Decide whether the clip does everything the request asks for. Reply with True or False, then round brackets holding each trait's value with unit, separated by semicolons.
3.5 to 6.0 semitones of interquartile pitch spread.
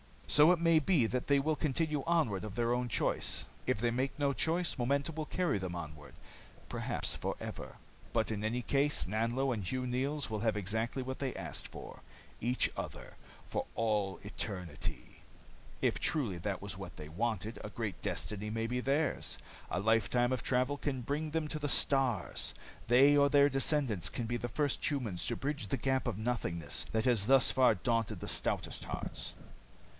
True (4.7 semitones)